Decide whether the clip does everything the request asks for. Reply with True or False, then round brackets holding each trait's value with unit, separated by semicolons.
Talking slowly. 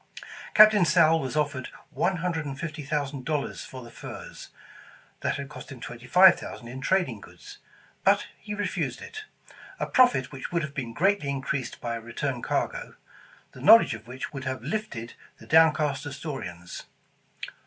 False (165 wpm)